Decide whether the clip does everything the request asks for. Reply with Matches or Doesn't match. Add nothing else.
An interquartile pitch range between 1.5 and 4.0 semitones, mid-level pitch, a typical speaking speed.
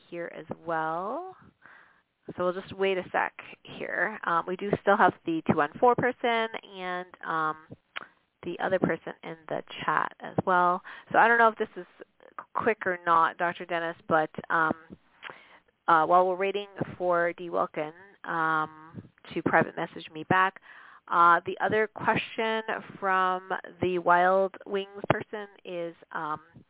Matches